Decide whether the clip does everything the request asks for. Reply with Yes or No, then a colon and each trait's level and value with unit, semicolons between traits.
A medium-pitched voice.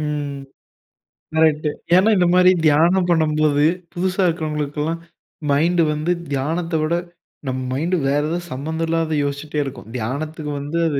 Yes: medium, 155 Hz